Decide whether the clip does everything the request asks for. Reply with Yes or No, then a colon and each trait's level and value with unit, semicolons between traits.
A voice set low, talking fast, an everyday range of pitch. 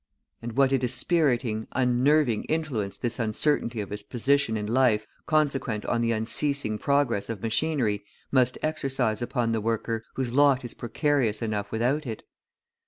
No: low, 120 Hz; average, 150 wpm; average, 4.0 semitones